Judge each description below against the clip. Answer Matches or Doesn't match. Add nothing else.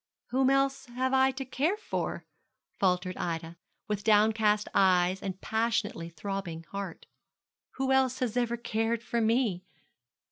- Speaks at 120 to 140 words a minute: Matches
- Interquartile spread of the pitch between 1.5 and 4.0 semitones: Doesn't match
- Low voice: Doesn't match